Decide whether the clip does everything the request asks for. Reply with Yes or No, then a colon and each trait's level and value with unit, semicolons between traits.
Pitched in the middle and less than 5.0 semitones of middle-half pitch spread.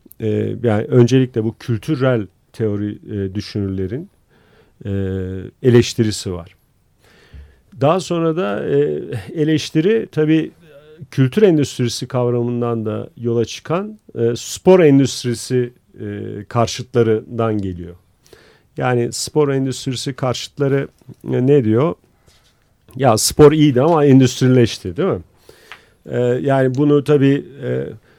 No: low, 125 Hz; average, 4.5 semitones